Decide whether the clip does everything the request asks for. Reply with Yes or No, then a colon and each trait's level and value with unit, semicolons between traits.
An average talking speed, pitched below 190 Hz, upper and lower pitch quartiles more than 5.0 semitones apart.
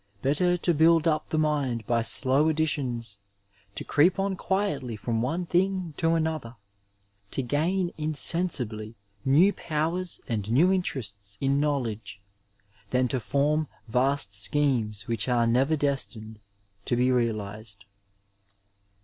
No: slow, 125 wpm; medium, 140 Hz; wide, 5.6 semitones